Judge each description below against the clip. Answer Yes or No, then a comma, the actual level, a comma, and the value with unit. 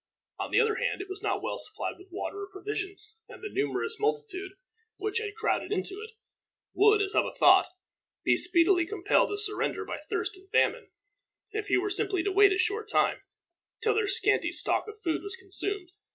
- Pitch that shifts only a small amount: Yes, narrow, 1.9 semitones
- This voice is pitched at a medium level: No, very high, 405 Hz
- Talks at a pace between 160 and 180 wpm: No, average, 195 wpm